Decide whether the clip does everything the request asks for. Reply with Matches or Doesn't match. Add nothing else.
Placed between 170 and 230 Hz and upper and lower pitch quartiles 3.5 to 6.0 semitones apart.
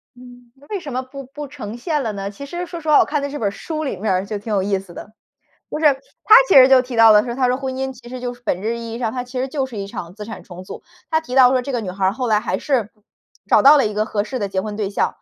Doesn't match